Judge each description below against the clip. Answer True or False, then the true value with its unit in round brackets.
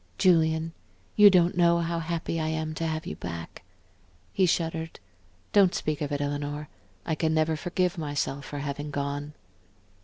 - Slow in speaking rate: False (160 wpm)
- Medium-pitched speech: True (160 Hz)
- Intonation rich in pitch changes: False (2.6 semitones)